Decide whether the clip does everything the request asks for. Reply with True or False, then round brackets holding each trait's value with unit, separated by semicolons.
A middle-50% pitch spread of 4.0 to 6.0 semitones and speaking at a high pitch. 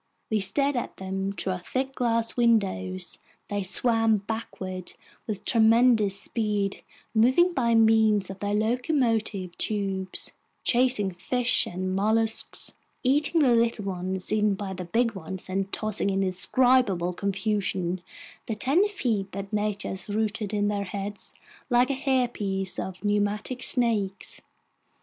False (3.4 semitones; 210 Hz)